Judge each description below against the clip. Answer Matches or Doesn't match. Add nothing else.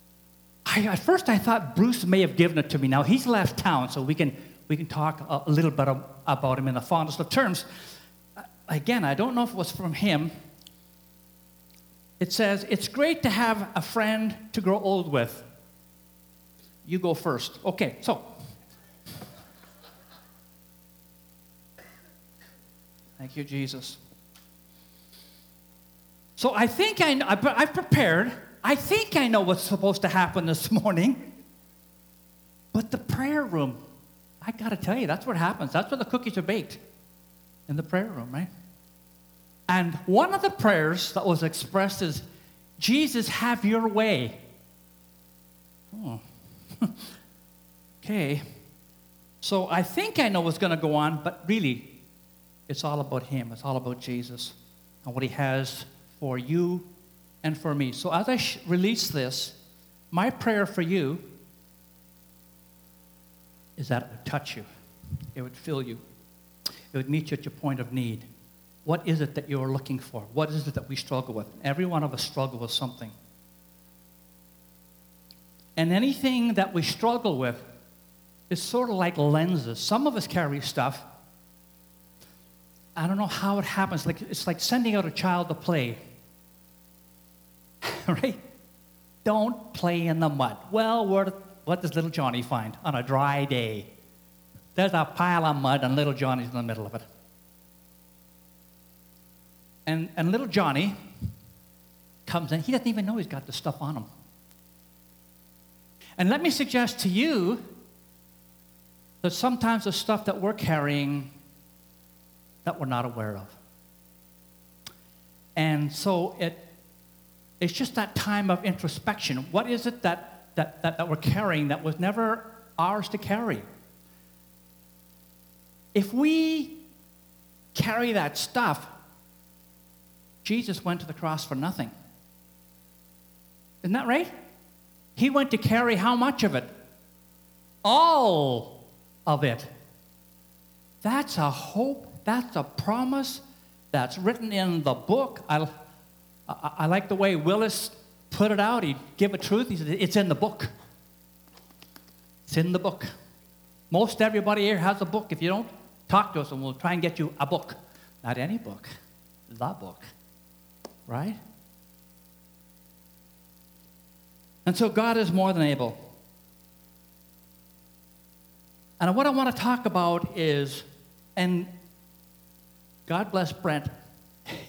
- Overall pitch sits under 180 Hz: Matches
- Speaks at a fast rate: Doesn't match